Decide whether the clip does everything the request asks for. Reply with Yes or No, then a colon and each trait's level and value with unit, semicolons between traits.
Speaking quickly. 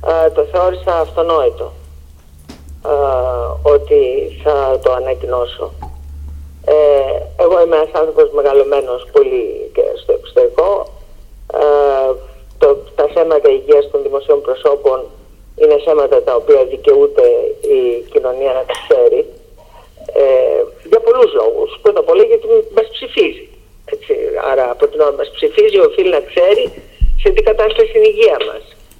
No: average, 130 wpm